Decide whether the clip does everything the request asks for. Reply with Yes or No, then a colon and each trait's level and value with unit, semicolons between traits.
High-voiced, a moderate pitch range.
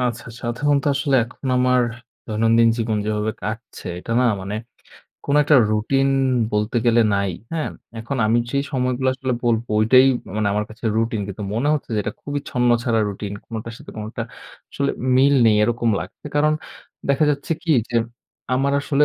No: low, 120 Hz; average, 3.9 semitones